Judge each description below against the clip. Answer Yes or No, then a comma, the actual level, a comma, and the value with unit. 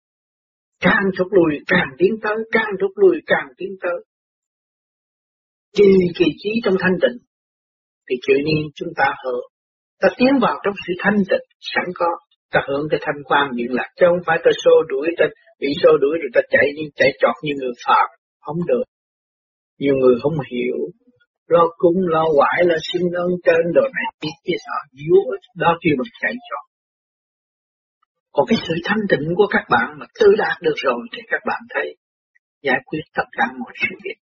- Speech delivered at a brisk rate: No, average, 190 wpm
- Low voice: No, high, 200 Hz